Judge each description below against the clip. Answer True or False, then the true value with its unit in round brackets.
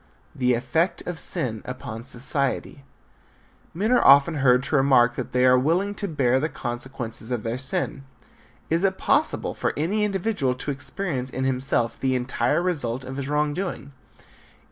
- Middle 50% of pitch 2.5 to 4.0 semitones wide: False (4.5 semitones)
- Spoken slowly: False (165 wpm)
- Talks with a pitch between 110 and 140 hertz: True (135 Hz)